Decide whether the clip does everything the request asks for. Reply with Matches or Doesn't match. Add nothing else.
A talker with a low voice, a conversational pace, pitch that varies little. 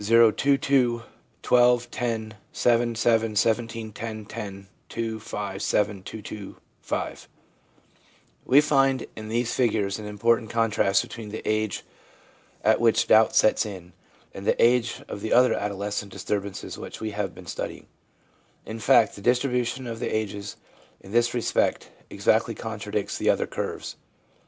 Matches